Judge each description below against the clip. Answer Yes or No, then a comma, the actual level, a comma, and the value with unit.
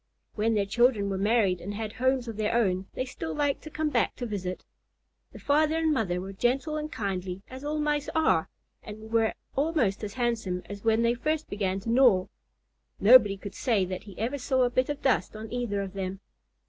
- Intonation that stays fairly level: No, average, 4.8 semitones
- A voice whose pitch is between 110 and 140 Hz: No, high, 225 Hz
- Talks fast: Yes, fast, 210 wpm